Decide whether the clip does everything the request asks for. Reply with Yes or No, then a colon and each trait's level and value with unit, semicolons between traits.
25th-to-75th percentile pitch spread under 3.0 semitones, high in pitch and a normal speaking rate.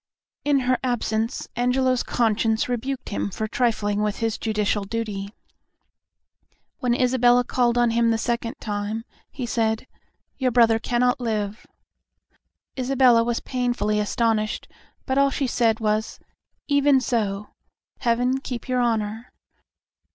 No: narrow, 2.4 semitones; high, 235 Hz; slow, 125 wpm